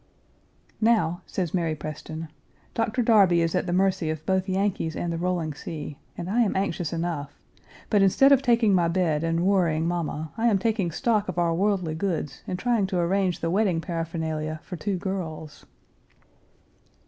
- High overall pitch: No, medium, 175 Hz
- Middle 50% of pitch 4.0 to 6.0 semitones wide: No, average, 3.2 semitones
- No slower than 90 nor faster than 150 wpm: No, average, 170 wpm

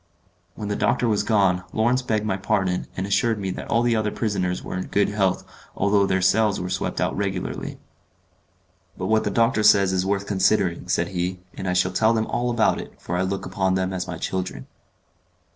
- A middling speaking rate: No, fast, 210 wpm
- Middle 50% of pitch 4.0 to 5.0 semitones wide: No, average, 2.7 semitones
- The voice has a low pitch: Yes, low, 100 Hz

